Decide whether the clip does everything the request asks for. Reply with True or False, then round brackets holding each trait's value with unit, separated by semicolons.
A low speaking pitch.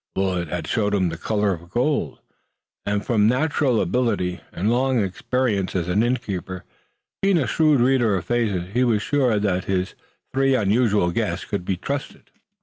True (105 Hz)